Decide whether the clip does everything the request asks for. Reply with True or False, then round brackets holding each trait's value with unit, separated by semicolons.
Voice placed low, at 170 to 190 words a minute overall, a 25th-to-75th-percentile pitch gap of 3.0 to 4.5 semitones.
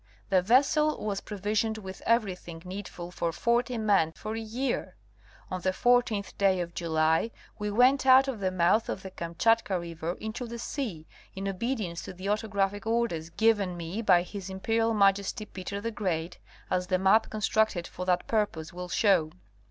False (200 Hz; 175 wpm; 3.8 semitones)